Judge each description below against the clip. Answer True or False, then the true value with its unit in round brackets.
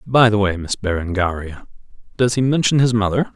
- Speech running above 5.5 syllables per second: False (5.4 syllables/s)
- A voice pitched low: True (105 Hz)